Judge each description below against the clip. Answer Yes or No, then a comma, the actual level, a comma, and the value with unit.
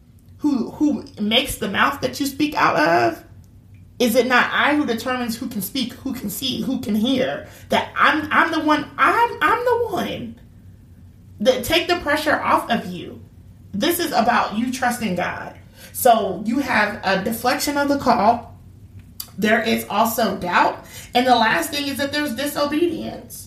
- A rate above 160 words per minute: Yes, average, 170 wpm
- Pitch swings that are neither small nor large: No, wide, 6.0 semitones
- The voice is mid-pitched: No, high, 245 Hz